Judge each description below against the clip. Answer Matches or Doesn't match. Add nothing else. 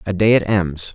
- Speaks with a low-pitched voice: Matches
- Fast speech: Matches